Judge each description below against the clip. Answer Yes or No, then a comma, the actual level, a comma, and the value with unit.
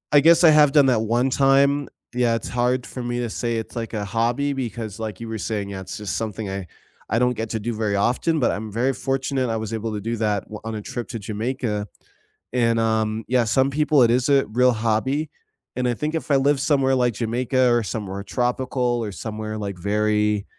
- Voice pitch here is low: Yes, low, 115 Hz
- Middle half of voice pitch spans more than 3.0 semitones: Yes, average, 3.4 semitones